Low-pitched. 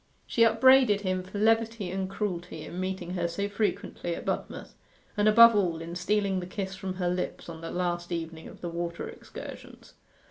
No: medium, 185 Hz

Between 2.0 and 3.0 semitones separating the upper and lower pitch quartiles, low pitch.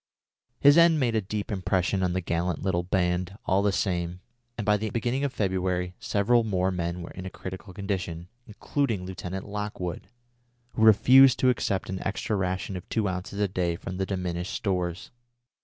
Yes: average, 2.7 semitones; very low, 95 Hz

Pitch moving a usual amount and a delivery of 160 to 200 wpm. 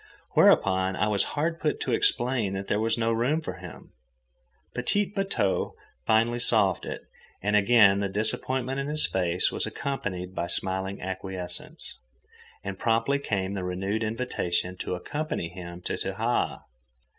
No: average, 4.8 semitones; average, 145 wpm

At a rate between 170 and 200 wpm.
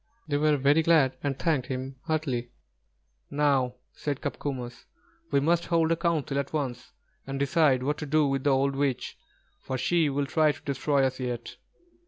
Yes: average, 175 wpm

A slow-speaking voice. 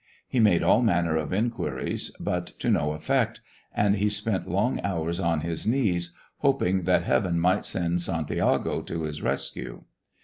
No: average, 160 wpm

